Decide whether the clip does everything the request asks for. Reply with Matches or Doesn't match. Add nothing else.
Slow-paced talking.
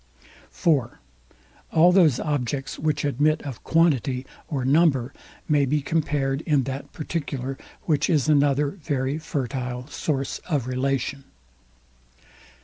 Matches